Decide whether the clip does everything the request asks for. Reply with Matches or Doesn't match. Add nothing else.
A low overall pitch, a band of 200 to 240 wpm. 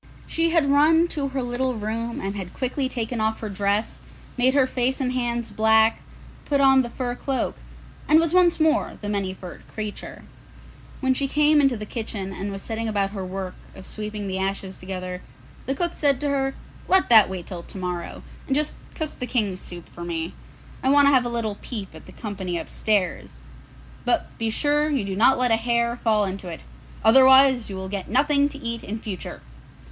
Doesn't match